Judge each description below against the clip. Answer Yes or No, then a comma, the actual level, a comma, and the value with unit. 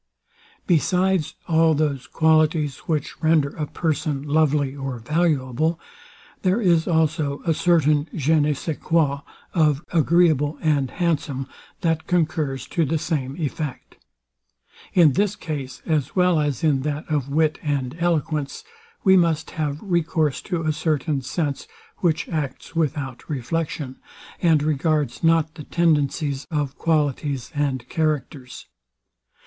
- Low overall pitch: No, medium, 155 Hz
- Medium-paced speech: No, slow, 130 wpm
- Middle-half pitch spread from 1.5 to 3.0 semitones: Yes, narrow, 2.6 semitones